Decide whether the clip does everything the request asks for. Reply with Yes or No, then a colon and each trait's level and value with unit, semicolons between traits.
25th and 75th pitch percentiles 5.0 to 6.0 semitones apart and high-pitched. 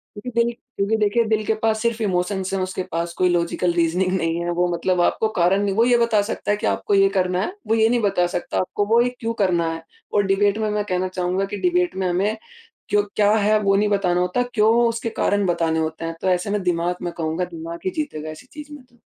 No: average, 3.4 semitones; high, 195 Hz